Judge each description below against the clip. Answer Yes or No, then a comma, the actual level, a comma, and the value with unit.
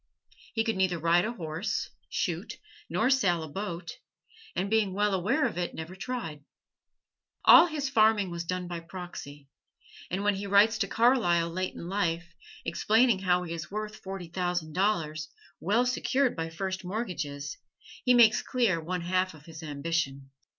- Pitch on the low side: No, medium, 185 Hz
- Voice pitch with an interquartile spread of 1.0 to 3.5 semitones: No, average, 4.3 semitones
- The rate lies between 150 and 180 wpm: Yes, average, 165 wpm